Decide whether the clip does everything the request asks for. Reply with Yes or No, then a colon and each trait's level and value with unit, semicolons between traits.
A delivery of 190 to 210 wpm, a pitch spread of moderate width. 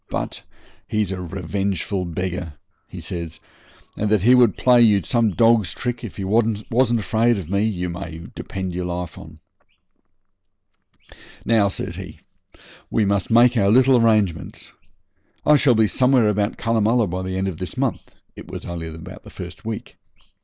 No: average, 160 wpm; average, 4.1 semitones